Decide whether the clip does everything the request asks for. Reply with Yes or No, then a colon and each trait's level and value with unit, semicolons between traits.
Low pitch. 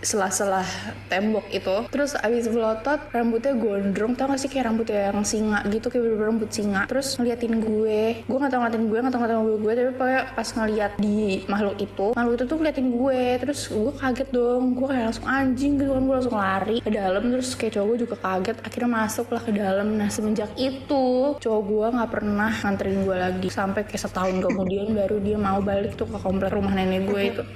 No: high, 220 Hz